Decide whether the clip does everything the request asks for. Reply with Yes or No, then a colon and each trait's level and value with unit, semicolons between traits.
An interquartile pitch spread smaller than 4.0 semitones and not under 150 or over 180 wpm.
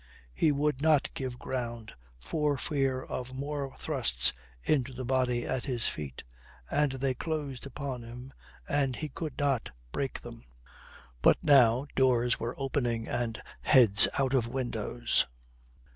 No: narrow, 2.6 semitones; average, 140 wpm